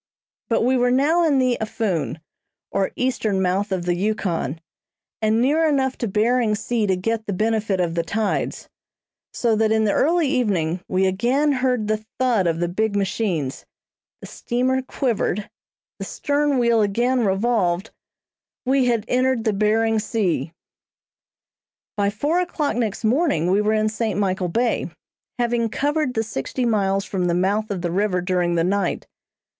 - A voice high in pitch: Yes, high, 220 Hz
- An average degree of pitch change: Yes, average, 4.5 semitones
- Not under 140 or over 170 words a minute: Yes, average, 160 wpm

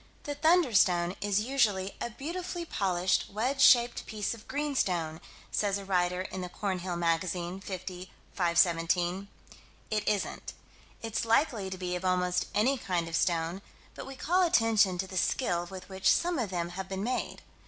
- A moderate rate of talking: Yes, average, 165 wpm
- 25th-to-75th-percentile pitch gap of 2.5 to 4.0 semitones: No, average, 4.4 semitones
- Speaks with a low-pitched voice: No, high, 190 Hz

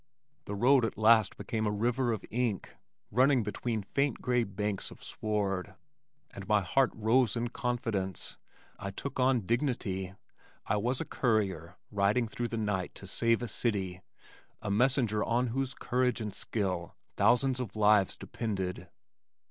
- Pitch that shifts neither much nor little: Yes, average, 3.6 semitones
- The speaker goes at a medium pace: Yes, average, 150 wpm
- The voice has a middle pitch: No, low, 110 Hz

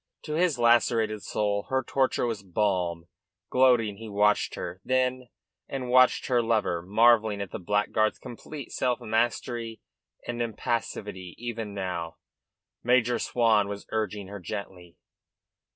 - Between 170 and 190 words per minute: No, slow, 135 wpm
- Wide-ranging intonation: No, average, 3.1 semitones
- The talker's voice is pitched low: Yes, low, 110 Hz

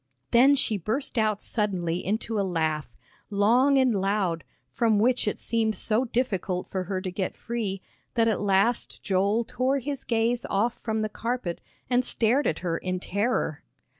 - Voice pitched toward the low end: No, high, 215 Hz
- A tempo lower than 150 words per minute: No, average, 165 wpm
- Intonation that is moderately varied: Yes, average, 3.9 semitones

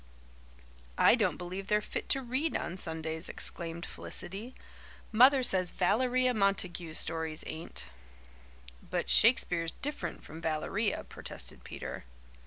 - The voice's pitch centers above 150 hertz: Yes, medium, 185 Hz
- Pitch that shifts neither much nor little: No, wide, 6.4 semitones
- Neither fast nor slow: No, slow, 115 wpm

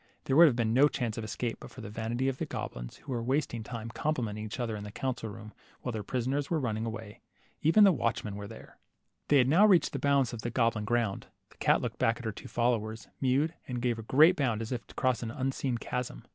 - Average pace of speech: No, fast, 255 wpm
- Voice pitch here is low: Yes, low, 120 Hz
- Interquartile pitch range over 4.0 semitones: No, average, 3.2 semitones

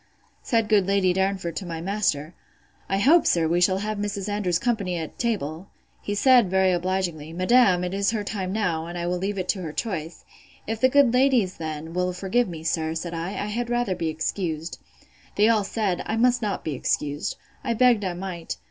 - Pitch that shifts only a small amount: No, average, 3.8 semitones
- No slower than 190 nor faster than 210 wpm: Yes, fast, 205 wpm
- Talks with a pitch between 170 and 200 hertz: Yes, high, 190 Hz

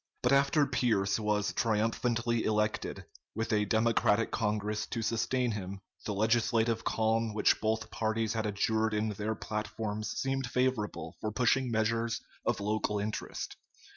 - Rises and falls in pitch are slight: Yes, narrow, 1.5 semitones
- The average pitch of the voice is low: Yes, low, 110 Hz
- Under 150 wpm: Yes, average, 140 wpm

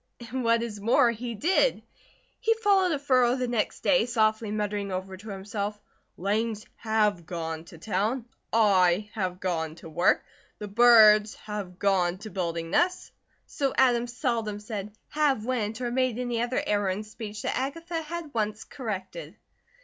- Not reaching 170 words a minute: Yes, average, 160 wpm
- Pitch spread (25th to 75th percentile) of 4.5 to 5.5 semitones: No, average, 3.8 semitones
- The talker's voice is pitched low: No, high, 215 Hz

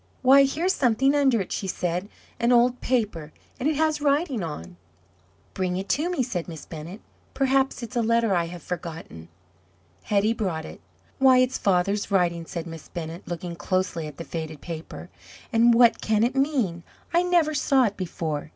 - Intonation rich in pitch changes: Yes, wide, 7.4 semitones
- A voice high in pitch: Yes, high, 210 Hz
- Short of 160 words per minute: No, average, 180 wpm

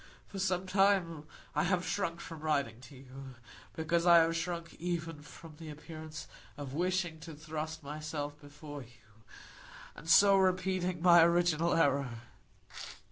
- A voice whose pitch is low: No, medium, 160 Hz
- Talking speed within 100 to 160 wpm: Yes, average, 140 wpm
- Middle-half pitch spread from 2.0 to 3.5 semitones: Yes, average, 3.0 semitones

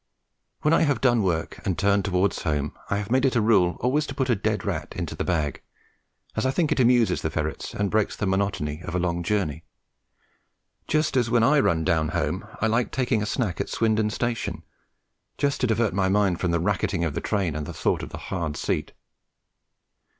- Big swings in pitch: Yes, wide, 5.7 semitones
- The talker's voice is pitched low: Yes, low, 100 Hz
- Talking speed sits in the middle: No, fast, 215 wpm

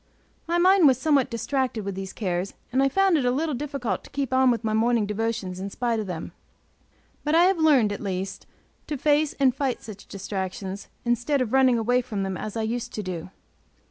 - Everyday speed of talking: No, fast, 210 wpm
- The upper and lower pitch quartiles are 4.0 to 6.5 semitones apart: Yes, average, 5.3 semitones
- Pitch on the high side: Yes, high, 240 Hz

